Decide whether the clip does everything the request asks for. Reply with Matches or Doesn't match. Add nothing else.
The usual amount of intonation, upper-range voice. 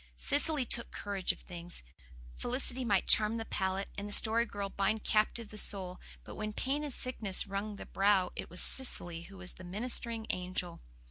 Matches